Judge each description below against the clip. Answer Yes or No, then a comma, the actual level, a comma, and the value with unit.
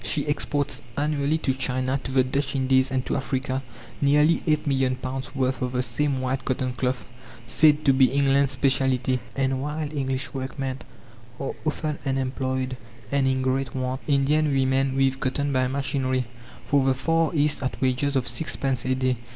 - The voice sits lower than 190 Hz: Yes, low, 135 Hz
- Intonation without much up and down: Yes, narrow, 1.4 semitones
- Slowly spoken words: No, average, 175 wpm